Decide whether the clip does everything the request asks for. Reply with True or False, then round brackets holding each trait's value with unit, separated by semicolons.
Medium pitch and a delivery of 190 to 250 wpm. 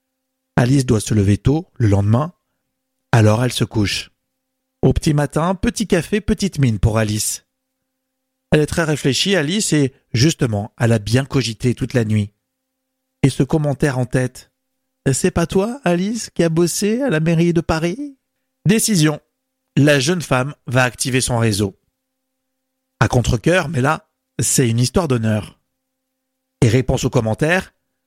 False (155 Hz; 150 wpm)